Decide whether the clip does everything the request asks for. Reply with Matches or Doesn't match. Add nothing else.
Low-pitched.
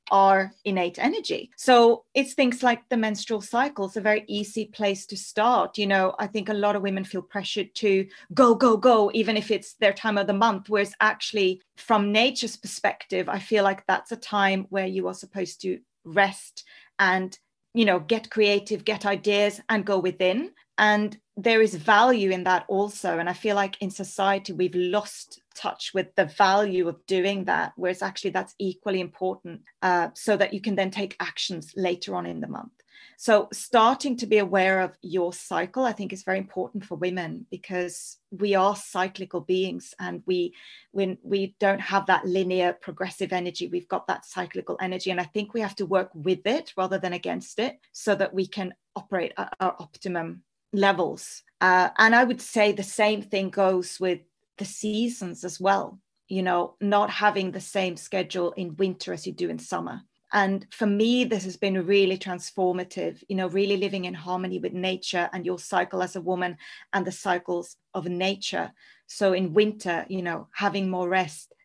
Doesn't match